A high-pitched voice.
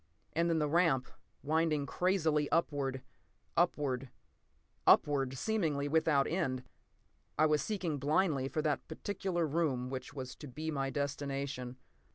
No: medium, 150 Hz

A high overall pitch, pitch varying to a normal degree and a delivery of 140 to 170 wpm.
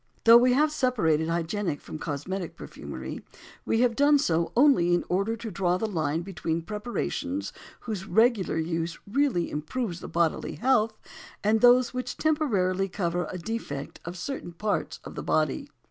No: high, 195 Hz; wide, 6.2 semitones; average, 160 wpm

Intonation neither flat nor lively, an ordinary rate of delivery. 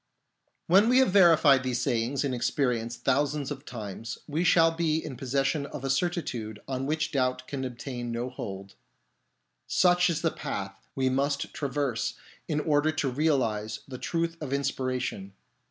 Yes: average, 3.9 semitones; average, 165 wpm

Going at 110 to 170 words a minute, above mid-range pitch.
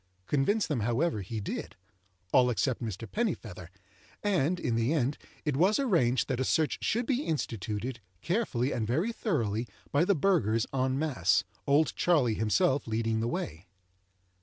No: average, 150 wpm; low, 130 Hz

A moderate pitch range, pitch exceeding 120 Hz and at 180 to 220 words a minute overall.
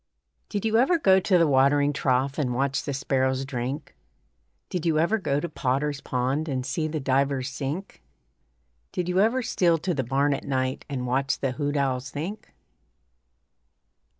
No: average, 4.0 semitones; medium, 140 Hz; average, 170 wpm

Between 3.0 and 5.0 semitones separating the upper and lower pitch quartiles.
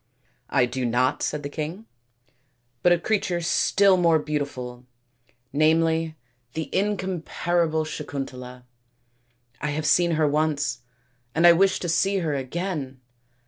Yes: average, 4.4 semitones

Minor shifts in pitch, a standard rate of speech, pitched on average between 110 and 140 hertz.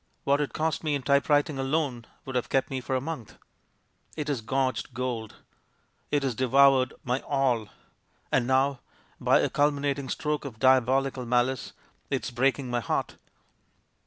Yes: narrow, 2.1 semitones; average, 160 wpm; low, 135 Hz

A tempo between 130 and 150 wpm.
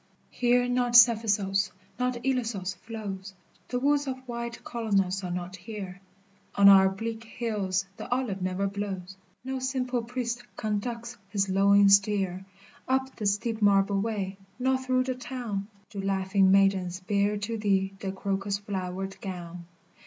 Yes: average, 145 wpm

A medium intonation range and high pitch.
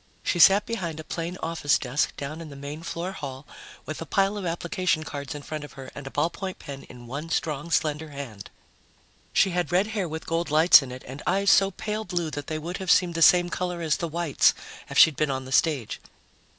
No: average, 3.6 semitones; medium, 160 Hz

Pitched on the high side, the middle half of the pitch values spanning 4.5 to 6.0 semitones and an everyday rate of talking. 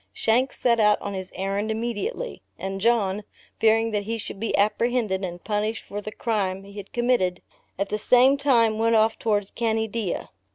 No: high, 215 Hz; narrow, 2.5 semitones; average, 175 wpm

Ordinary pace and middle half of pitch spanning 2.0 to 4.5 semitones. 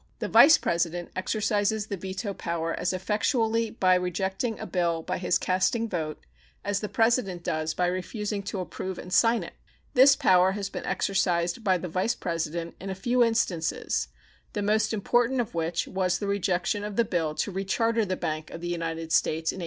Yes: average, 190 wpm; average, 3.7 semitones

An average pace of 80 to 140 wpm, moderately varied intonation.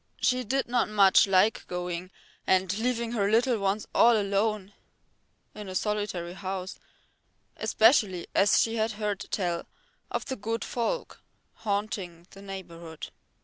Yes: slow, 135 wpm; average, 3.1 semitones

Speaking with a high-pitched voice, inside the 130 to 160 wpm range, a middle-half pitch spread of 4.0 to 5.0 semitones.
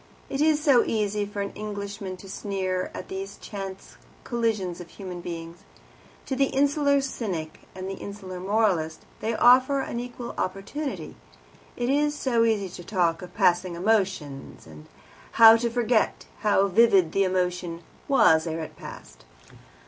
Yes: high, 200 Hz; average, 150 wpm; average, 4.7 semitones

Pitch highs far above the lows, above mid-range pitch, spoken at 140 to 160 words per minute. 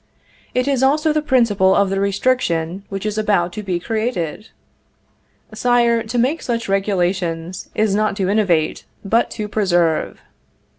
No: average, 4.0 semitones; high, 210 Hz; average, 145 wpm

